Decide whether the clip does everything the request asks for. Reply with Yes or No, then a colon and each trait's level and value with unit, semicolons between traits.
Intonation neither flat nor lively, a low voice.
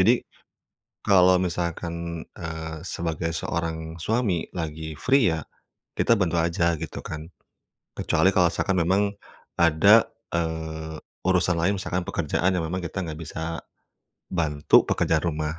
No: narrow, 2.2 semitones; very low, 85 Hz